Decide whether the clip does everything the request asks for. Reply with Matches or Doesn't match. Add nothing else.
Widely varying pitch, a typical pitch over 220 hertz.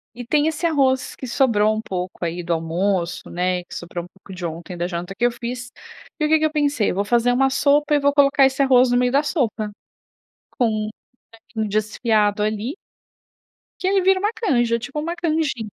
Matches